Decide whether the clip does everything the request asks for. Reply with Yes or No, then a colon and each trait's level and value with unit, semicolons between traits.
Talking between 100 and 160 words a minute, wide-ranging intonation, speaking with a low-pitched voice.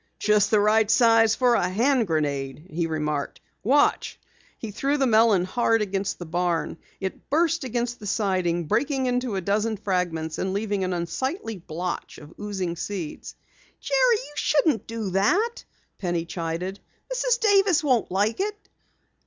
No: average, 155 wpm; wide, 6.1 semitones; high, 210 Hz